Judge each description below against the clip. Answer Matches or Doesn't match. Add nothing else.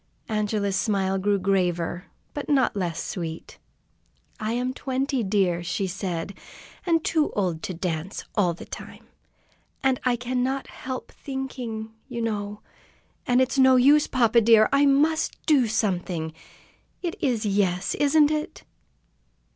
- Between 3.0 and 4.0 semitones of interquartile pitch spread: Doesn't match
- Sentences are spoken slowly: Matches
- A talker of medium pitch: Doesn't match